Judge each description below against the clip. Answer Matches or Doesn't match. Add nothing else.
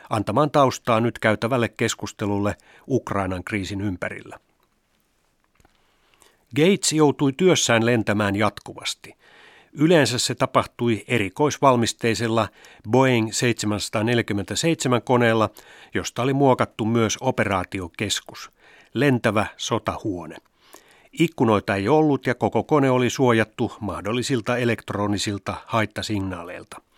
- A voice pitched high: Doesn't match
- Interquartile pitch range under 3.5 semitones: Doesn't match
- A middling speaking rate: Doesn't match